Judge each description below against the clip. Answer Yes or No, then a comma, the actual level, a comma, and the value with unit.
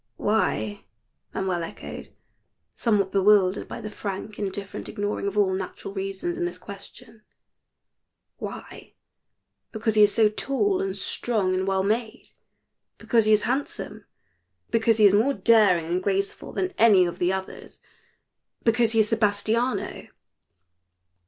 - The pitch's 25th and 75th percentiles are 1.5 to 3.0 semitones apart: Yes, average, 2.7 semitones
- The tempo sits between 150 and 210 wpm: No, average, 140 wpm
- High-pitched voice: Yes, high, 205 Hz